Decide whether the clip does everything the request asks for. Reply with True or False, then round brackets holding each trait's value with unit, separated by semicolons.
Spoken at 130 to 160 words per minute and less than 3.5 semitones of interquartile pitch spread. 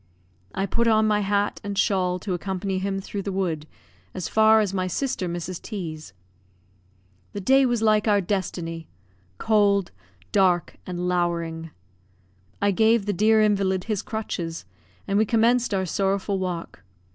True (155 wpm; 2.9 semitones)